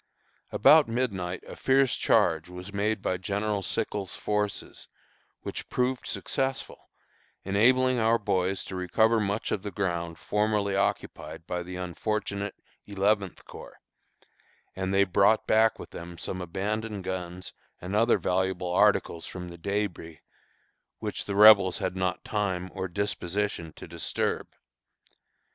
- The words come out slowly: Yes, slow, 130 wpm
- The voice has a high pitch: No, low, 100 Hz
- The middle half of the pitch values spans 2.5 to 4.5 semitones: Yes, average, 2.9 semitones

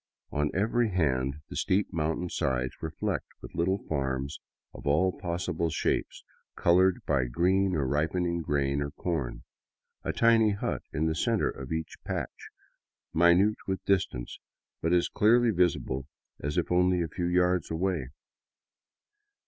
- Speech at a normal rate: Yes, average, 145 wpm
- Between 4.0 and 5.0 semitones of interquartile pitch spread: Yes, average, 4.3 semitones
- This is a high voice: No, very low, 85 Hz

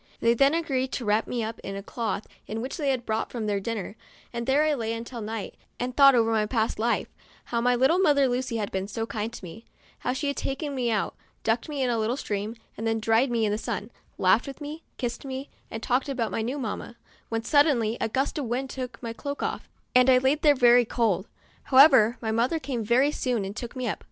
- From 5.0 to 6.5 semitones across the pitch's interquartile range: No, average, 3.1 semitones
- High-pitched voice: Yes, high, 240 Hz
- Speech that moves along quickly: Yes, fast, 240 wpm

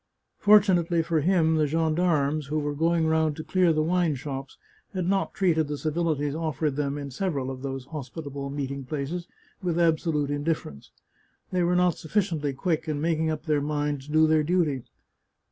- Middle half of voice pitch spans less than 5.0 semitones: Yes, average, 2.7 semitones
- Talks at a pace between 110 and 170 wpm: No, average, 180 wpm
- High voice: No, medium, 155 Hz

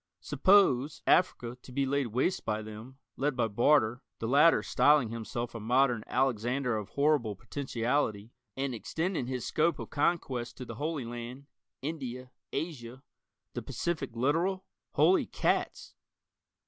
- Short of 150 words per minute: Yes, slow, 135 wpm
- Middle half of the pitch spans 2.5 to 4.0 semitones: Yes, average, 3.7 semitones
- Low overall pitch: Yes, low, 130 Hz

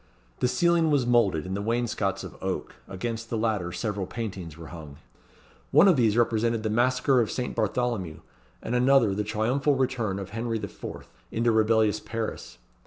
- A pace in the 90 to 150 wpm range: No, average, 170 wpm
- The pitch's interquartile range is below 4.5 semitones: Yes, average, 3.3 semitones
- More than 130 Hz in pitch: No, low, 110 Hz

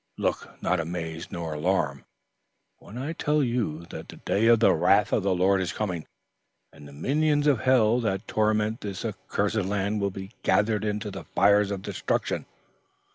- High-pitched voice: No, low, 100 Hz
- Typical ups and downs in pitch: Yes, average, 3.4 semitones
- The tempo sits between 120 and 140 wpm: No, average, 175 wpm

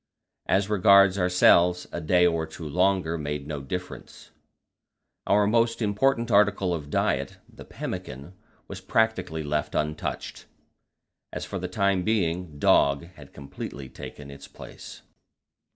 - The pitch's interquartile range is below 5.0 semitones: Yes, average, 4.6 semitones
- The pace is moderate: No, slow, 130 wpm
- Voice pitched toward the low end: Yes, very low, 90 Hz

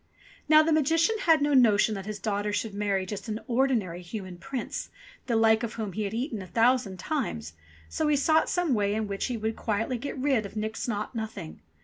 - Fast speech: Yes, fast, 215 wpm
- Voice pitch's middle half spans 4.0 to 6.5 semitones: Yes, average, 4.5 semitones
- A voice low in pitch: No, high, 220 Hz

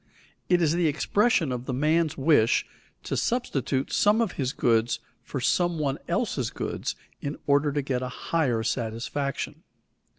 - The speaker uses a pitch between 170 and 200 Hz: No, medium, 140 Hz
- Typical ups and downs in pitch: Yes, average, 4.6 semitones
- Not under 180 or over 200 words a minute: No, average, 160 wpm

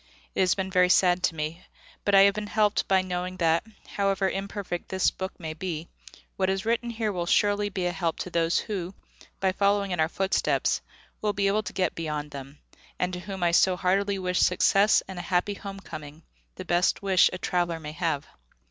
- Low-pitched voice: No, medium, 185 Hz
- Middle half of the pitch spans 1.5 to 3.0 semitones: Yes, narrow, 2.4 semitones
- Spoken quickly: Yes, fast, 210 wpm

